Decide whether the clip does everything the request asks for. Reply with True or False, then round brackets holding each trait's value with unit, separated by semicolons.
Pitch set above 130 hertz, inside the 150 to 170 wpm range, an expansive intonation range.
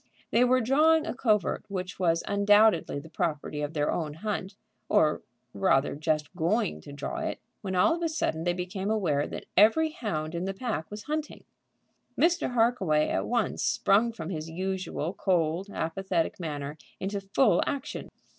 True (190 Hz; 165 wpm; 5.7 semitones)